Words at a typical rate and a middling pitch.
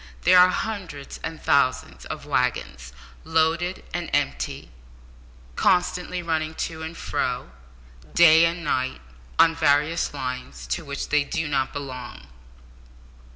No: slow, 120 wpm; medium, 160 Hz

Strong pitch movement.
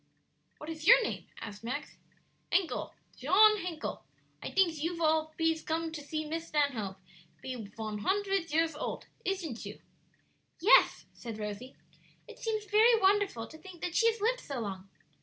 Yes: wide, 6.8 semitones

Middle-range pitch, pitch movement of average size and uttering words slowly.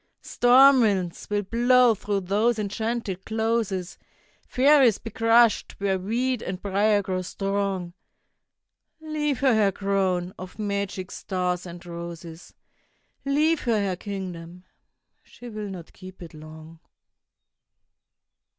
No: high, 200 Hz; average, 4.0 semitones; slow, 115 wpm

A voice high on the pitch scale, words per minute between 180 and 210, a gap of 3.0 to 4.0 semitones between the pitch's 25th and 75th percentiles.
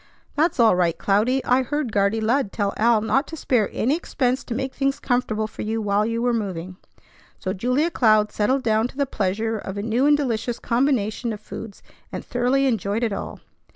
Yes: high, 230 Hz; average, 200 wpm; average, 3.7 semitones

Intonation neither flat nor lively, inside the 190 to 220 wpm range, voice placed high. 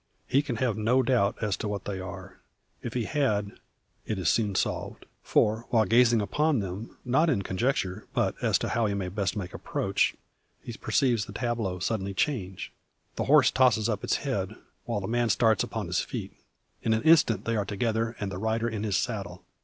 No: average, 3.3 semitones; average, 200 wpm; low, 110 Hz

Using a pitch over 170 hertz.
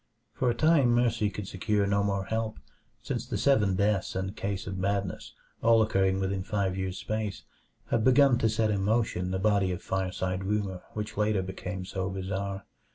No: low, 100 Hz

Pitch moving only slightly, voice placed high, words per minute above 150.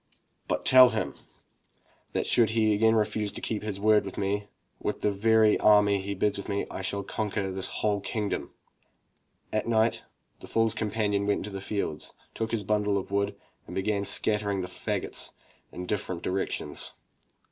No: narrow, 1.5 semitones; low, 105 Hz; average, 175 wpm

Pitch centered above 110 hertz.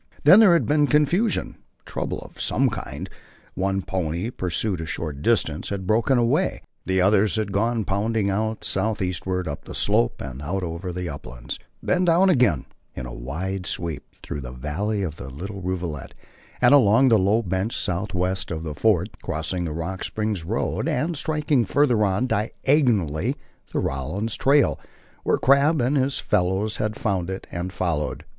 No: very low, 95 Hz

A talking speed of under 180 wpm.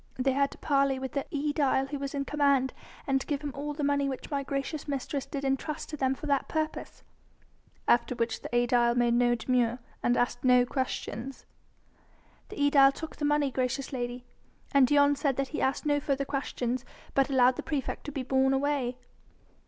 No: average, 195 wpm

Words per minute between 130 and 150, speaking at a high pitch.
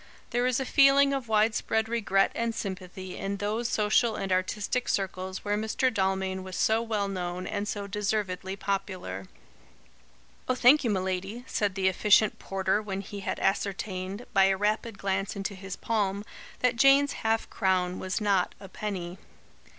No: average, 165 wpm; high, 200 Hz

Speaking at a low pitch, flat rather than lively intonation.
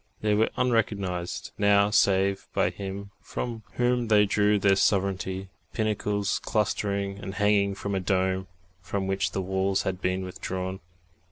Yes: low, 100 Hz; narrow, 1.5 semitones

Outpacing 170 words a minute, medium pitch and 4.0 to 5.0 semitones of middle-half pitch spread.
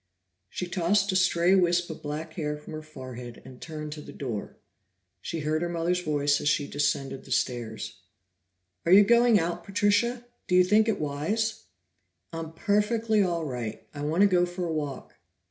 Yes: average, 185 wpm; medium, 165 Hz; average, 4.7 semitones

